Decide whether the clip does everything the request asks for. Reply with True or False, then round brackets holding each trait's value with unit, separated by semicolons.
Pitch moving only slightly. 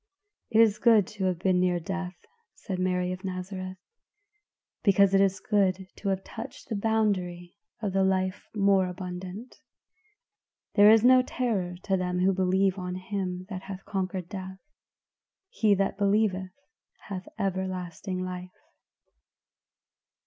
True (1.5 semitones)